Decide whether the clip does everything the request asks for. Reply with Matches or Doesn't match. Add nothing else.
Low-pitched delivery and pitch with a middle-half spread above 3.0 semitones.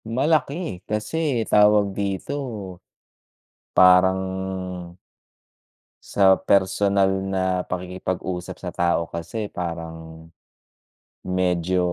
Doesn't match